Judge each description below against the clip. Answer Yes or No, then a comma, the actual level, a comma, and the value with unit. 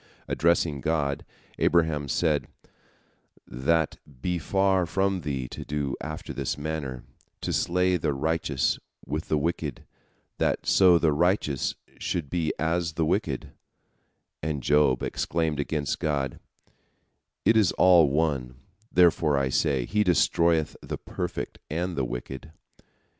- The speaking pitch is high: No, very low, 80 Hz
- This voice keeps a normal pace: No, slow, 125 wpm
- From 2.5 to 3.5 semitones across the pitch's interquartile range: Yes, average, 3.2 semitones